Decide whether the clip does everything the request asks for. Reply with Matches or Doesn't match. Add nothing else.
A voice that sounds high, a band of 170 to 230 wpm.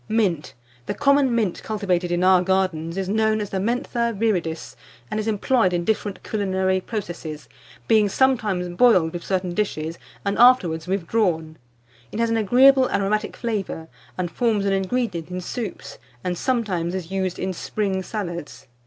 Doesn't match